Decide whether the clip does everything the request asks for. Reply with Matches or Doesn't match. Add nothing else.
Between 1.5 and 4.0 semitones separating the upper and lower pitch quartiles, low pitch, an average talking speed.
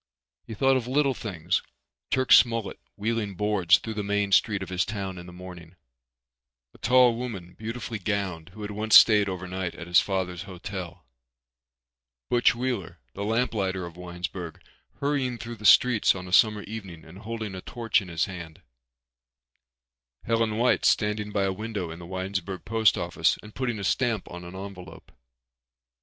Matches